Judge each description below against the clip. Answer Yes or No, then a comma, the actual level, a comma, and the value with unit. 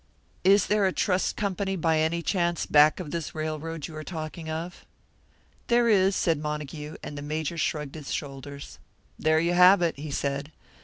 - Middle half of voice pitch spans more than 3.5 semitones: No, average, 3.1 semitones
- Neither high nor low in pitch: Yes, medium, 160 Hz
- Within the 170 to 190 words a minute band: Yes, average, 175 wpm